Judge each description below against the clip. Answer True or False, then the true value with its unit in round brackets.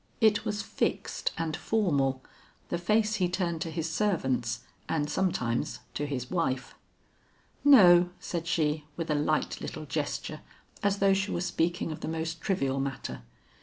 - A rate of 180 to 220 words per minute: False (155 wpm)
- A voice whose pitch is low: False (165 Hz)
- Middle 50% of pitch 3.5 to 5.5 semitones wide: True (4.4 semitones)